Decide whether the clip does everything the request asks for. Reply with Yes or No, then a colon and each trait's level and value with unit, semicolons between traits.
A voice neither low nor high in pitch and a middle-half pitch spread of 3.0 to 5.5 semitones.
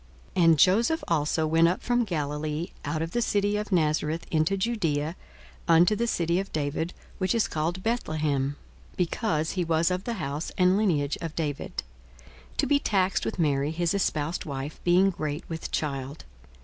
Yes: medium, 165 Hz; average, 3.9 semitones